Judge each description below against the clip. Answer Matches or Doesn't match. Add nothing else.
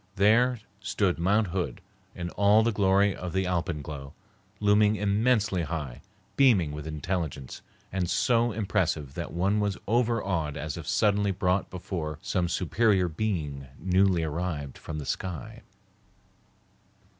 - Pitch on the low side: Matches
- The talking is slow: Matches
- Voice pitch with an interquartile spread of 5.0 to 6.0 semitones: Doesn't match